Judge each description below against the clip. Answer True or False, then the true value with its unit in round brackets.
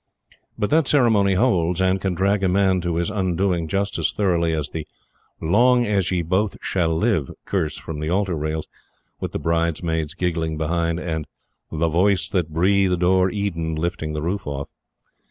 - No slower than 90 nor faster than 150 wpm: False (175 wpm)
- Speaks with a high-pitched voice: False (90 Hz)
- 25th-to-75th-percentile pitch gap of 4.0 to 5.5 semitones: False (3.3 semitones)